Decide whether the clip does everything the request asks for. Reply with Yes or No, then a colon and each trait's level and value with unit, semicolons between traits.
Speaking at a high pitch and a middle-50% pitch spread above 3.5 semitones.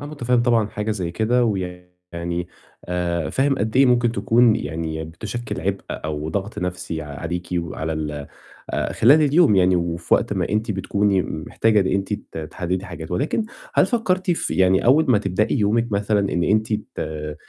No: very low, 95 Hz; average, 5.2 semitones